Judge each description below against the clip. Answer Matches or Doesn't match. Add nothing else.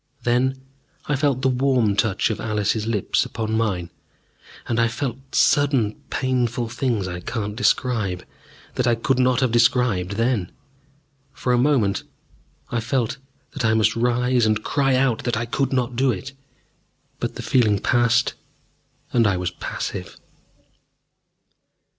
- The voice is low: Matches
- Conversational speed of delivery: Matches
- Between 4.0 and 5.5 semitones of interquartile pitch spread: Doesn't match